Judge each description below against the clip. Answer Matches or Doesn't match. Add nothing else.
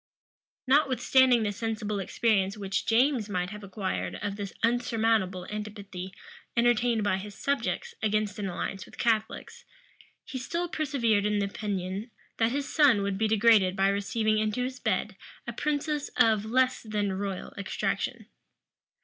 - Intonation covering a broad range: Doesn't match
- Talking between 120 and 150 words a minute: Matches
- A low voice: Doesn't match